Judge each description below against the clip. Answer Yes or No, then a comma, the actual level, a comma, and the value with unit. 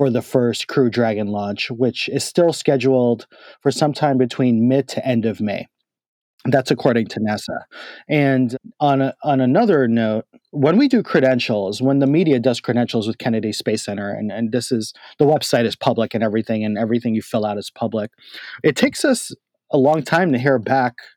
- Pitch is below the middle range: Yes, low, 125 Hz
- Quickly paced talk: No, average, 190 wpm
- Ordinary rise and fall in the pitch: Yes, average, 3.5 semitones